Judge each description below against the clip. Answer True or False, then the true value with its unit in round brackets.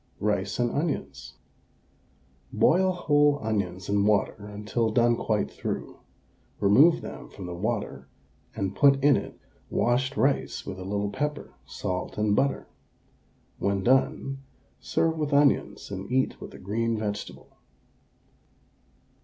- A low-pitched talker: True (110 Hz)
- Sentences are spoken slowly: True (130 wpm)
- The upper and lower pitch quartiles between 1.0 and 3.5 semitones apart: False (5.5 semitones)